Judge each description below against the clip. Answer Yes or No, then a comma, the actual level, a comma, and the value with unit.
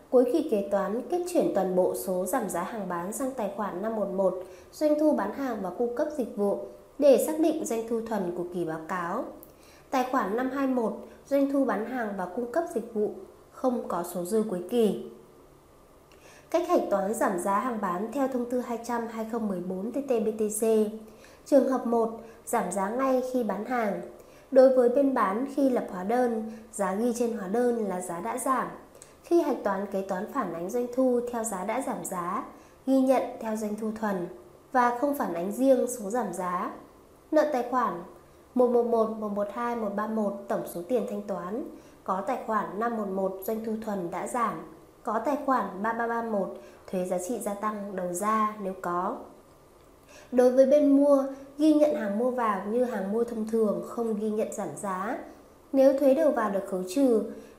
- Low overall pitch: No, high, 230 Hz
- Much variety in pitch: No, average, 4.4 semitones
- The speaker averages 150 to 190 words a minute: Yes, average, 185 wpm